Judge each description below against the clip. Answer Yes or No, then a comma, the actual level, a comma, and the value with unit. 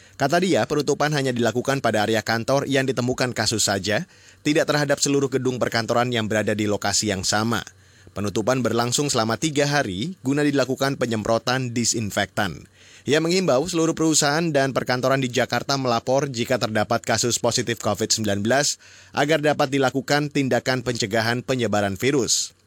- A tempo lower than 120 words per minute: No, fast, 140 wpm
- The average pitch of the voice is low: Yes, low, 125 Hz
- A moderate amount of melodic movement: Yes, average, 3.8 semitones